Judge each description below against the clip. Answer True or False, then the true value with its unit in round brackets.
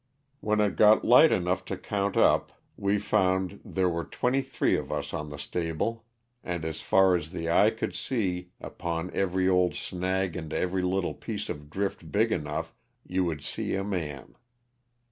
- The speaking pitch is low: True (90 Hz)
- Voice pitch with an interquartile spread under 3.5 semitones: True (3.1 semitones)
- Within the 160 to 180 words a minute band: False (200 wpm)